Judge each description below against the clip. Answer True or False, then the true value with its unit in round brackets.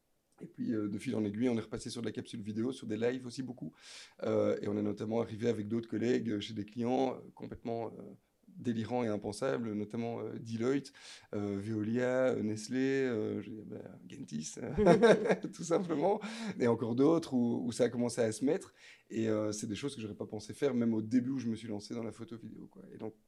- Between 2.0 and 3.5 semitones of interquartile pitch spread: True (2.7 semitones)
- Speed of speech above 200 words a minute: True (220 wpm)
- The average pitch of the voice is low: True (115 Hz)